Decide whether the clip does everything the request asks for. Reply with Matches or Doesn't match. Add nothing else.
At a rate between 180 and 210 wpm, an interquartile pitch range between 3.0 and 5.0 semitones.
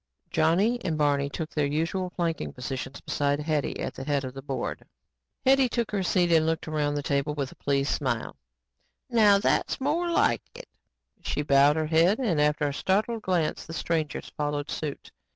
Matches